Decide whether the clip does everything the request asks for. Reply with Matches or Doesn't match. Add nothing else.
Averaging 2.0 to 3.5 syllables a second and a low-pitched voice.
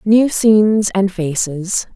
Doesn't match